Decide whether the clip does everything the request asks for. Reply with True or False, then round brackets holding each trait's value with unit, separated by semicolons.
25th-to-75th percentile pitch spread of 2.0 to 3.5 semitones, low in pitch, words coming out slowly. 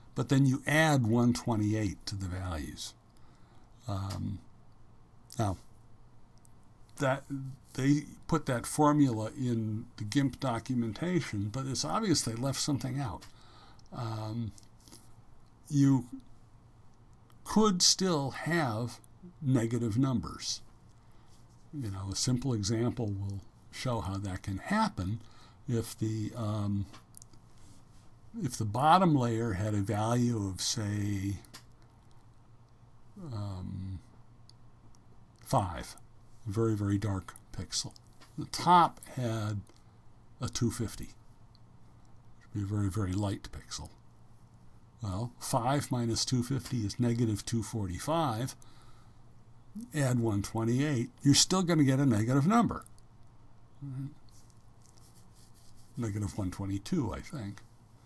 True (2.4 semitones; 115 Hz; 105 wpm)